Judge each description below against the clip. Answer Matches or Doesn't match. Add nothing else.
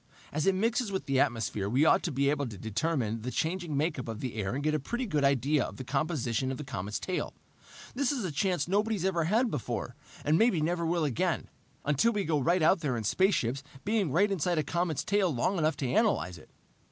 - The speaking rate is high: Matches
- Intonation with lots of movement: Matches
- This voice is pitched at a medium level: Matches